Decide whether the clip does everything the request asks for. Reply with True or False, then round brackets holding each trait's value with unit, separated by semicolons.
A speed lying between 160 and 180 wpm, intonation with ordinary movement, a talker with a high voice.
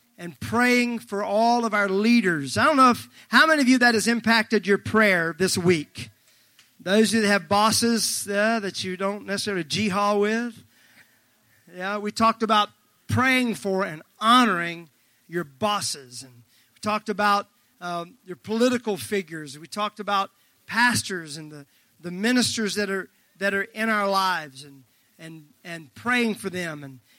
True (165 wpm; 4.4 semitones; 200 Hz)